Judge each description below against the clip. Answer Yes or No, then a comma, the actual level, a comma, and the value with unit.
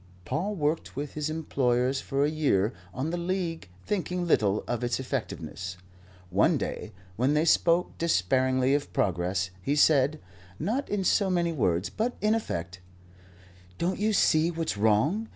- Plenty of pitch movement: Yes, wide, 6.9 semitones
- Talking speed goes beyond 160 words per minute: No, average, 150 wpm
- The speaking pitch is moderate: Yes, medium, 145 Hz